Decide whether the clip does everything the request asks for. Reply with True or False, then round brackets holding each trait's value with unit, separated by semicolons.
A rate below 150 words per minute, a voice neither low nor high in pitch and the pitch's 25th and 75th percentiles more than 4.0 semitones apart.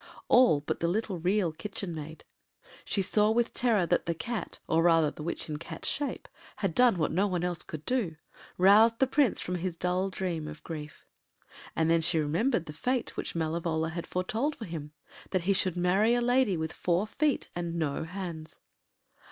False (185 wpm; 180 Hz; 4.7 semitones)